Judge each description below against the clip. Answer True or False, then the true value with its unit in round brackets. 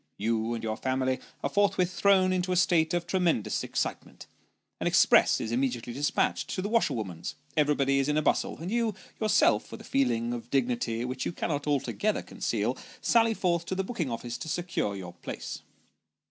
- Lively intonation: True (7.3 semitones)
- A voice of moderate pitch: True (145 Hz)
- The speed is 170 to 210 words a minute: True (185 wpm)